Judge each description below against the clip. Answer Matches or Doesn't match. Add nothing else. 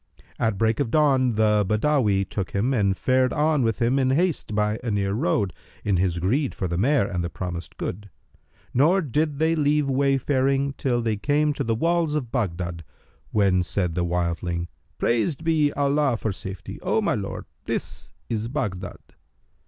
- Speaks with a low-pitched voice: Matches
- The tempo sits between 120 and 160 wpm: Doesn't match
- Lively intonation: Matches